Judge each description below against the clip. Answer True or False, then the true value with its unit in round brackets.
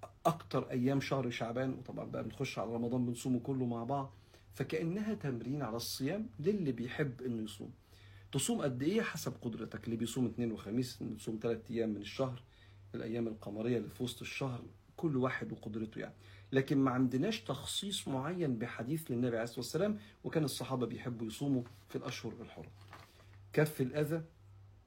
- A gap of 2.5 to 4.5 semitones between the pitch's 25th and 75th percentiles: True (3.2 semitones)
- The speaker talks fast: True (155 wpm)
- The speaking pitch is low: True (120 Hz)